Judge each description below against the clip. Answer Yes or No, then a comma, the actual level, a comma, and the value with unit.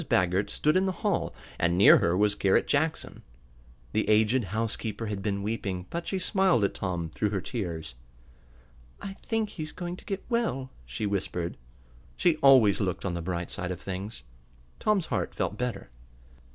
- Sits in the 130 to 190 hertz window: No, low, 105 Hz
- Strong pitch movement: Yes, wide, 9.0 semitones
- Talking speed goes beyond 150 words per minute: Yes, average, 170 wpm